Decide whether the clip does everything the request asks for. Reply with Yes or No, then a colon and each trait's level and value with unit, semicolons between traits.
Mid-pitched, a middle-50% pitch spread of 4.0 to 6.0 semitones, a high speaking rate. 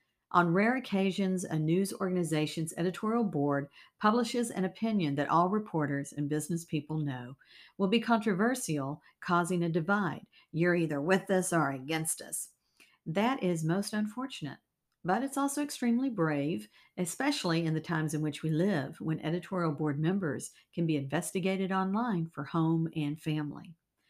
No: medium, 175 Hz; average, 4.3 semitones; average, 150 wpm